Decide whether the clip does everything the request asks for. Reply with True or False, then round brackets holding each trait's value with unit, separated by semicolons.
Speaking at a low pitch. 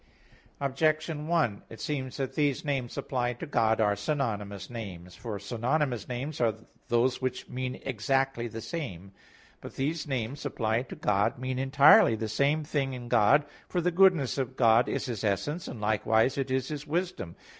True (130 Hz)